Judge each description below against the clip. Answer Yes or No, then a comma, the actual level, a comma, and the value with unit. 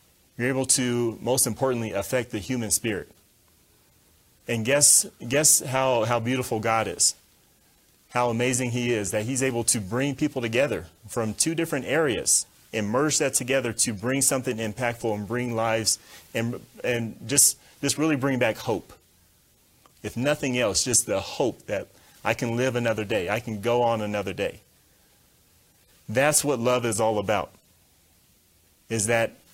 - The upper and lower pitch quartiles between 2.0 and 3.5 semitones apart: Yes, average, 3.0 semitones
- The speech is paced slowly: No, average, 155 wpm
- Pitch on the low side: Yes, low, 120 Hz